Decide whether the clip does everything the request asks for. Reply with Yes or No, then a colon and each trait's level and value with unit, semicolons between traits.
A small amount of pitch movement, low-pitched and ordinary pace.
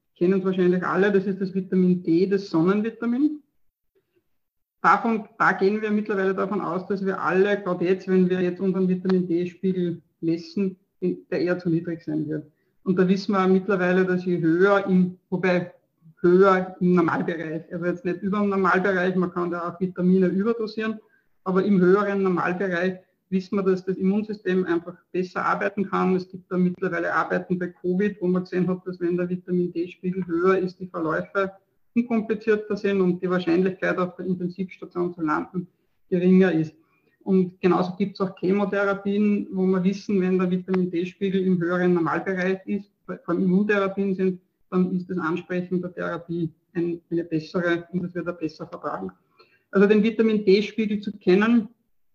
No: narrow, 1.7 semitones; medium, 185 Hz; average, 170 wpm